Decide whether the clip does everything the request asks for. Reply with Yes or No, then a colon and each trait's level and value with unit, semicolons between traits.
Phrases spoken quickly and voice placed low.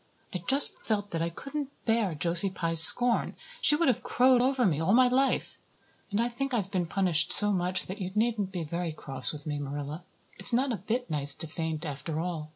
No: fast, 220 wpm; medium, 185 Hz